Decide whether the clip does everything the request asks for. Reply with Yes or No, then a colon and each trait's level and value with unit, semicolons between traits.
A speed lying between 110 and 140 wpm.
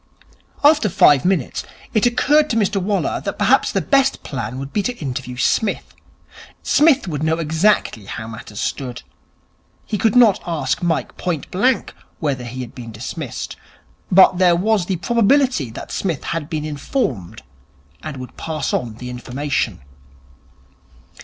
No: average, 150 wpm